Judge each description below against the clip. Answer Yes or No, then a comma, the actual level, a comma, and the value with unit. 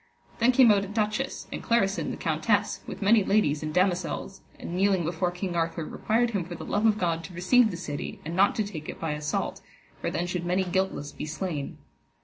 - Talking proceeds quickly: Yes, fast, 215 wpm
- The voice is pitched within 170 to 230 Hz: Yes, medium, 185 Hz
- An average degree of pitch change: Yes, average, 3.8 semitones